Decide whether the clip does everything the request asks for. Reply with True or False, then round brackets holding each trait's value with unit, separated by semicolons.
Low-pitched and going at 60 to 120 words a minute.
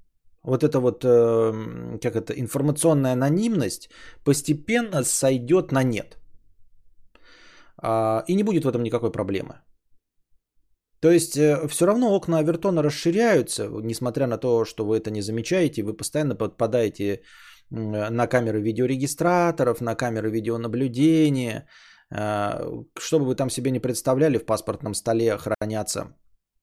True (120 Hz; 115 wpm)